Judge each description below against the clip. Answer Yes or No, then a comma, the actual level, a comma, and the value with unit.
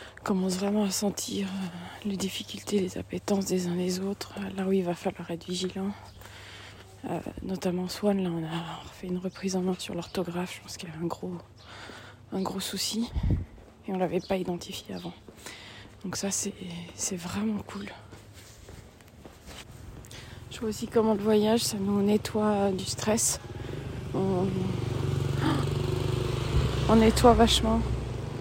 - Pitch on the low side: No, medium, 180 Hz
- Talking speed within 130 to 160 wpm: Yes, average, 155 wpm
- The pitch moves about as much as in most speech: No, wide, 8.2 semitones